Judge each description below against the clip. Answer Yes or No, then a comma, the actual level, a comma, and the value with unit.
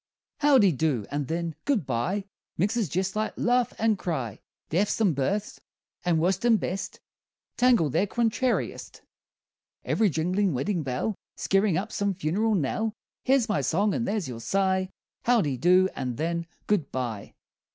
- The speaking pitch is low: No, high, 190 Hz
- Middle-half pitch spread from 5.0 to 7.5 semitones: Yes, average, 5.3 semitones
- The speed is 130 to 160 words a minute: Yes, average, 150 wpm